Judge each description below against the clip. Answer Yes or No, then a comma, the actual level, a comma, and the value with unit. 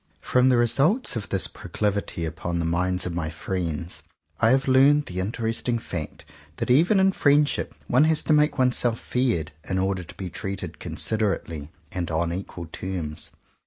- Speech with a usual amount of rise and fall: No, wide, 7.0 semitones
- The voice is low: Yes, low, 100 Hz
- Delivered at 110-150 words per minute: No, average, 165 wpm